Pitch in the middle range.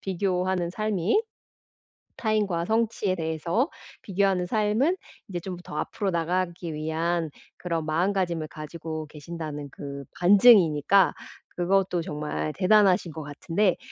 Yes: medium, 175 Hz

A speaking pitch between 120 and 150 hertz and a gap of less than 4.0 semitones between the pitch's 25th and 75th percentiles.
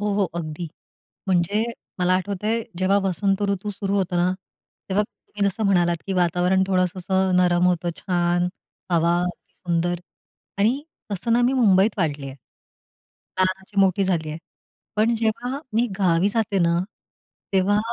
No: medium, 185 Hz; narrow, 2.5 semitones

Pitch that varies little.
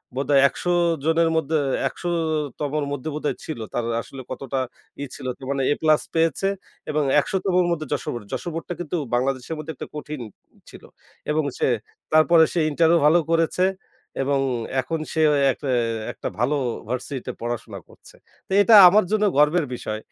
No: average, 3.4 semitones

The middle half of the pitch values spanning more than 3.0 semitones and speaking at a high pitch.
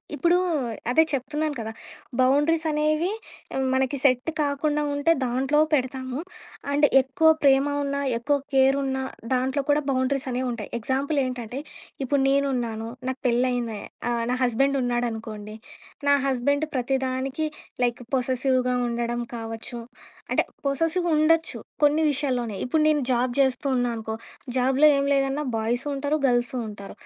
No: average, 2.7 semitones; very high, 265 Hz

